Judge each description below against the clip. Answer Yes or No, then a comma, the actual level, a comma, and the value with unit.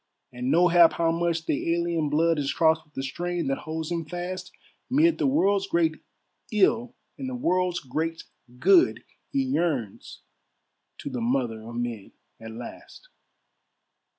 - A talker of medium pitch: Yes, medium, 165 Hz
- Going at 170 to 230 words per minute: No, average, 150 wpm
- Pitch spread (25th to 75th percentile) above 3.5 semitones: Yes, average, 4.7 semitones